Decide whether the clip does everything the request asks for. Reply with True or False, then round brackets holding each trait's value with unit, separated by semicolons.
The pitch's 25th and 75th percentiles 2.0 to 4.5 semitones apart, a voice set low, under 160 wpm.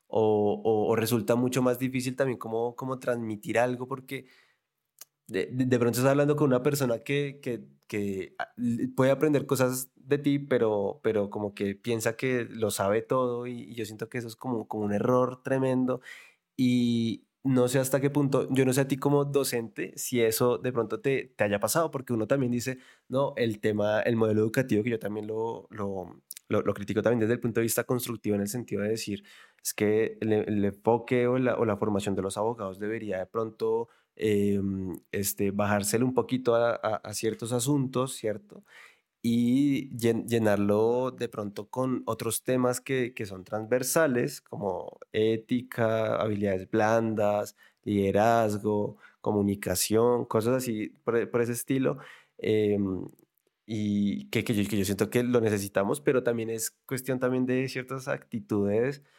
False (3.2 semitones; 115 Hz; 175 wpm)